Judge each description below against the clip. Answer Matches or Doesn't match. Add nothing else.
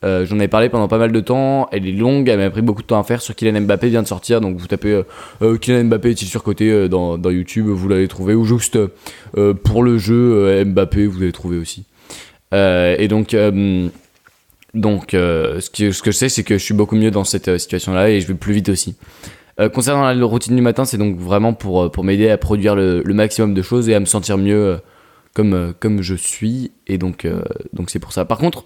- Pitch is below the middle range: Matches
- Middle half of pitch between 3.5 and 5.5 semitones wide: Doesn't match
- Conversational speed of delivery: Doesn't match